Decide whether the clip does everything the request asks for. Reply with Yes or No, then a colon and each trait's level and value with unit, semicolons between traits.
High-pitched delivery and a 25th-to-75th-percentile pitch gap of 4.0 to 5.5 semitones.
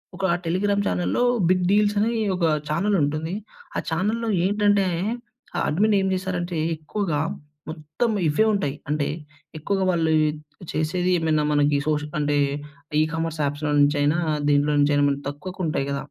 No: medium, 160 Hz; average, 4.7 semitones